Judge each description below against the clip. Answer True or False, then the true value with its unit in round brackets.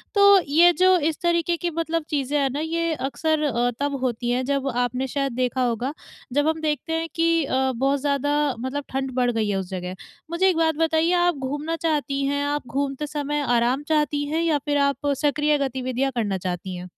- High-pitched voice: True (285 Hz)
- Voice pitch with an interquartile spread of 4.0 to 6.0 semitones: False (3.6 semitones)